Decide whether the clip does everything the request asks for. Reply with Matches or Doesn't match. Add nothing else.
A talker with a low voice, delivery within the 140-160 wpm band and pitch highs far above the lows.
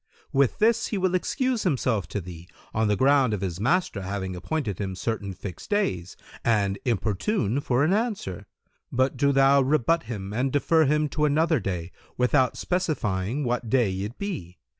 Doesn't match